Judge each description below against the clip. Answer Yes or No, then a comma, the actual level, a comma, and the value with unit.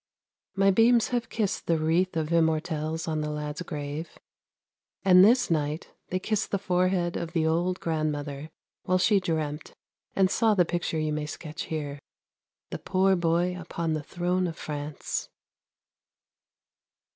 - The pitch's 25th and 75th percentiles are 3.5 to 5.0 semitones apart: No, average, 3.0 semitones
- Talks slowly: No, average, 150 wpm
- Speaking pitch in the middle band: Yes, medium, 165 Hz